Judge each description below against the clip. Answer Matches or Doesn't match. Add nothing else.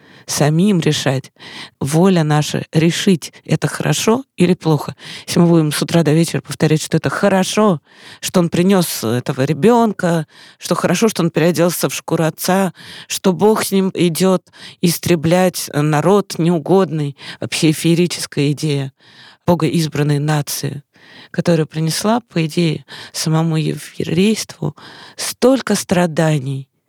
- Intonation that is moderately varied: Matches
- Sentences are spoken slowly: Doesn't match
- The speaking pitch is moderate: Matches